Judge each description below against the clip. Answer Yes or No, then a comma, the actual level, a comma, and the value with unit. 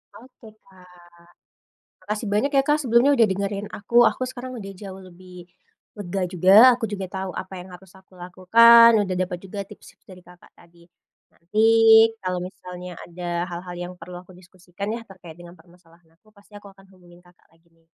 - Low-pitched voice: No, medium, 185 Hz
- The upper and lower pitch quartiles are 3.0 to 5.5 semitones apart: No, narrow, 2.5 semitones